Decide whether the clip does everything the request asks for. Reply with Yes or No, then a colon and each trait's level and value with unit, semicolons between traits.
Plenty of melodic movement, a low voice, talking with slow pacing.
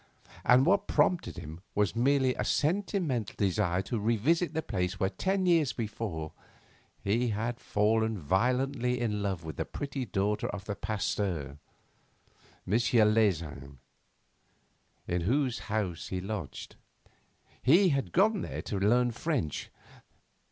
Yes: wide, 5.7 semitones; low, 110 Hz; slow, 130 wpm